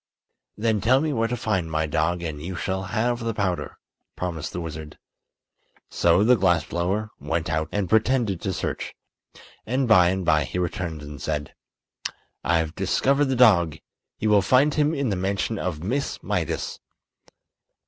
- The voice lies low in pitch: Yes, very low, 95 Hz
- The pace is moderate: Yes, average, 165 wpm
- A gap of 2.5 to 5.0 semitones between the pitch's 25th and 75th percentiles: No, wide, 5.5 semitones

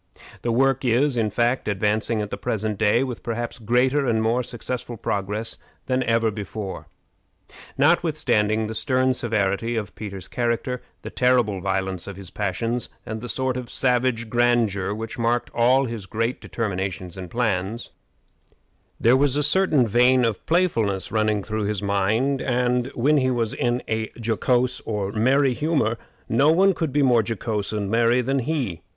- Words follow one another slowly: No, average, 160 wpm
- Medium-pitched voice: No, low, 115 Hz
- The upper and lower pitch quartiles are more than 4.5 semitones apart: No, average, 3.2 semitones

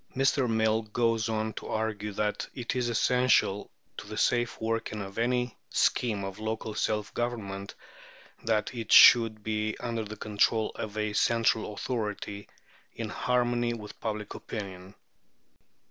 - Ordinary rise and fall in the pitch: No, narrow, 2.0 semitones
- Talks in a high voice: No, low, 110 Hz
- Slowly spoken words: No, average, 145 wpm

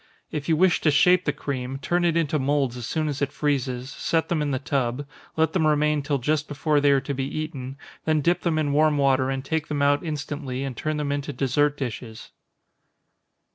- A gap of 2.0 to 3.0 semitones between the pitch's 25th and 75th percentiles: Yes, narrow, 2.4 semitones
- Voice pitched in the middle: Yes, medium, 145 Hz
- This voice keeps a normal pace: No, fast, 215 wpm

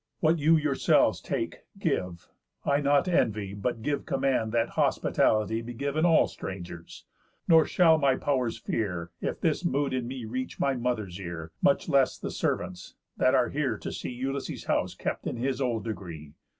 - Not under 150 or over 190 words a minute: Yes, average, 170 wpm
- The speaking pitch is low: Yes, low, 125 Hz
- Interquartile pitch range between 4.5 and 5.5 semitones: Yes, average, 5.1 semitones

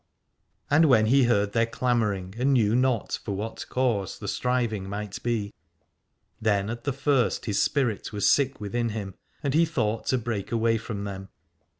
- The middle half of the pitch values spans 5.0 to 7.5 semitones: No, average, 3.6 semitones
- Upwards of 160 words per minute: Yes, average, 175 wpm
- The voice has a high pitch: No, low, 115 Hz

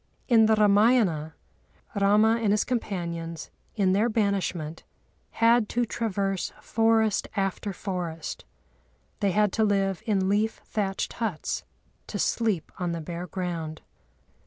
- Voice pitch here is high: Yes, high, 200 Hz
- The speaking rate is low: Yes, slow, 125 wpm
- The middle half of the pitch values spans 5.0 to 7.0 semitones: No, average, 3.7 semitones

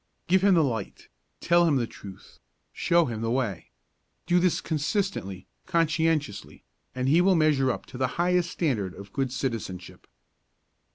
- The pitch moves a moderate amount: No, wide, 7.0 semitones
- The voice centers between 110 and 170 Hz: Yes, medium, 140 Hz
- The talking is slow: No, average, 155 wpm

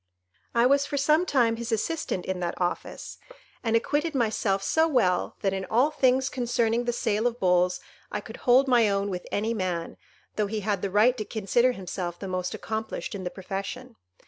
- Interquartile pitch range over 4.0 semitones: Yes, average, 4.4 semitones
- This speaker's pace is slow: No, average, 195 wpm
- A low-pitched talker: No, high, 220 Hz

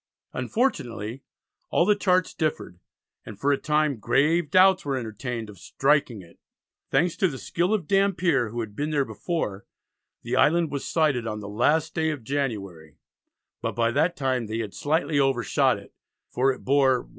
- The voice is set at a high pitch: No, medium, 140 Hz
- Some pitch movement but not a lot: No, wide, 5.8 semitones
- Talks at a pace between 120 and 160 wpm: No, average, 175 wpm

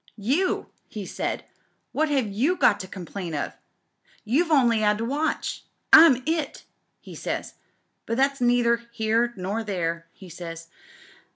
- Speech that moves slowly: No, average, 155 wpm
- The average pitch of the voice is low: No, high, 230 Hz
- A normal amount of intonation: No, wide, 5.9 semitones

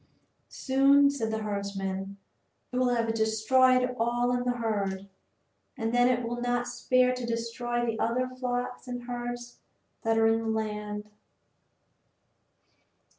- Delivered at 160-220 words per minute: No, slow, 135 wpm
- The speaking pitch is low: No, high, 240 Hz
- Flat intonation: Yes, narrow, 2.1 semitones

